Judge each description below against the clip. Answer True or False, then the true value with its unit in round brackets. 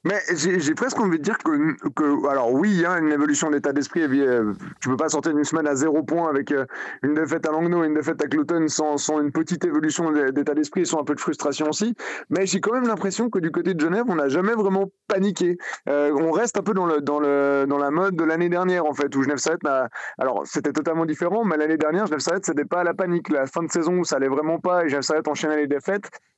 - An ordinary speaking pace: False (255 wpm)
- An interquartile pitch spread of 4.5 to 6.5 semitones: False (3.3 semitones)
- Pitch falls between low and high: True (160 Hz)